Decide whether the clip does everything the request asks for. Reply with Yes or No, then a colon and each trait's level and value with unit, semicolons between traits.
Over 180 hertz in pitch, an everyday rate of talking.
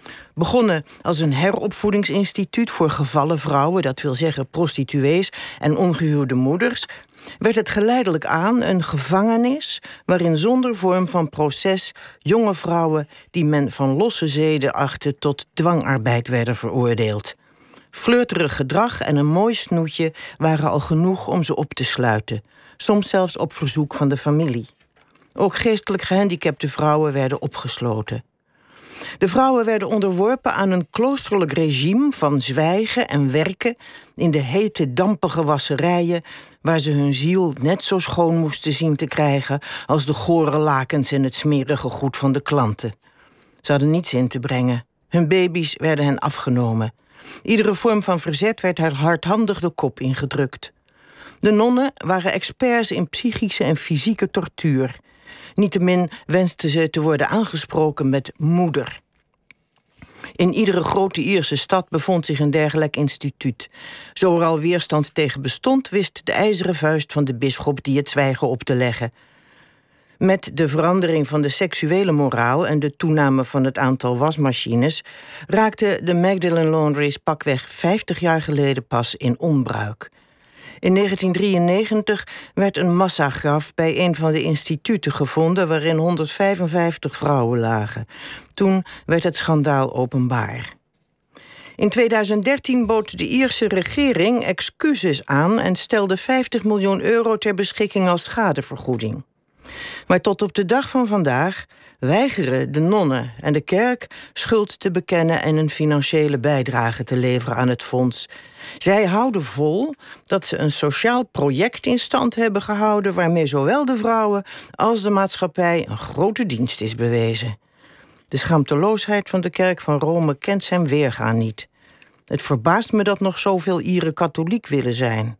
No: medium, 160 Hz; average, 145 wpm